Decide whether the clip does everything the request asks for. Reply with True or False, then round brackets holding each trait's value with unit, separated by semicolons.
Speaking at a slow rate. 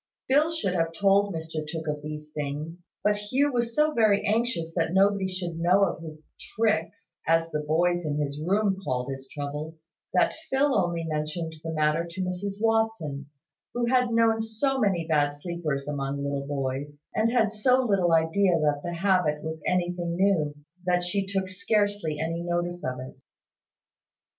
False (170 wpm)